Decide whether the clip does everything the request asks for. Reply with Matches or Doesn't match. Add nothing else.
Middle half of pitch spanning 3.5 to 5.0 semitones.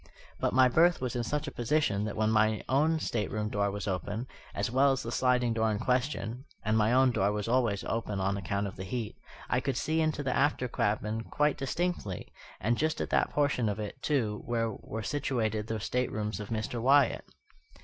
Matches